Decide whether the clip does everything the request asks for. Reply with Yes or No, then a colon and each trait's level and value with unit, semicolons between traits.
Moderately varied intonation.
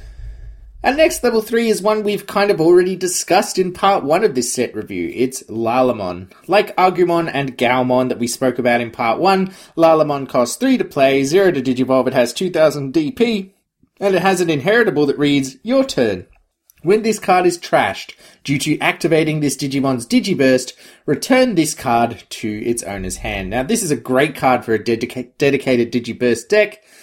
No: wide, 7.6 semitones